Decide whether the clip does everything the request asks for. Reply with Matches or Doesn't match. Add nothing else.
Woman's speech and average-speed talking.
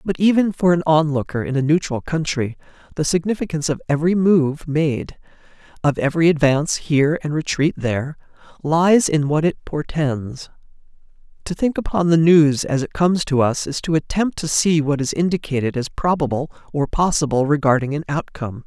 Doesn't match